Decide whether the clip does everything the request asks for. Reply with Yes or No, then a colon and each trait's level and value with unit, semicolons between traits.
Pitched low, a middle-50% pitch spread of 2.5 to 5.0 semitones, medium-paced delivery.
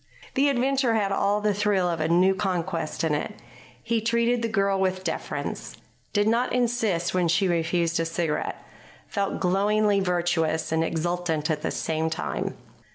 No: high, 190 Hz; average, 4.1 semitones; average, 160 wpm